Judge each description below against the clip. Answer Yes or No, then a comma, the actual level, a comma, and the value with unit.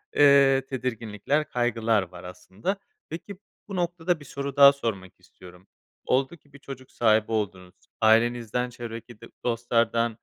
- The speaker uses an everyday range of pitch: Yes, average, 4.3 semitones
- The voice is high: No, low, 120 Hz